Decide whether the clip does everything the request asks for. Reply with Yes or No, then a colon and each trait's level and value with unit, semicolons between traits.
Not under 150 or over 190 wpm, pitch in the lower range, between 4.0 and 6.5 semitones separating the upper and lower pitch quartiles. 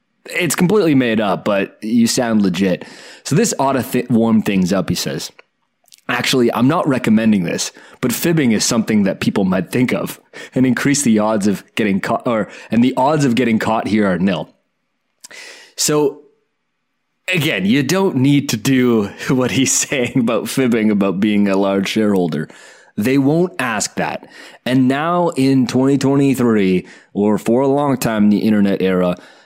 Yes: average, 175 wpm; low, 125 Hz; average, 4.9 semitones